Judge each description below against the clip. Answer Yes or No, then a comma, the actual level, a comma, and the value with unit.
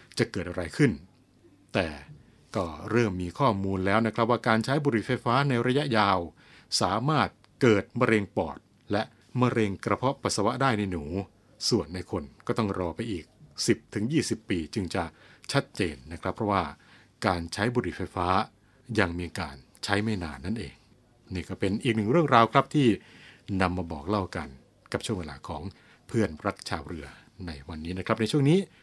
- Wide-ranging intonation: No, average, 4.4 semitones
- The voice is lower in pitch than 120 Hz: Yes, low, 105 Hz